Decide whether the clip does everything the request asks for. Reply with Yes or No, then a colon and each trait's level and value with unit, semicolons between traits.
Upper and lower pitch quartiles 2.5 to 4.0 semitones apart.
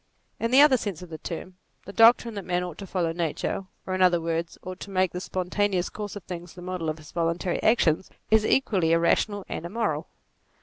Yes: average, 3.2 semitones